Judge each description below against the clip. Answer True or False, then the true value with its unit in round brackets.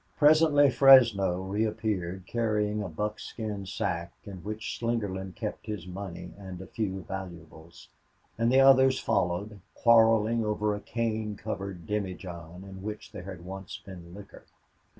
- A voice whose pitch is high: False (105 Hz)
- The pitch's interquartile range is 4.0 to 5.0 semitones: False (3.0 semitones)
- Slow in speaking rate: True (130 wpm)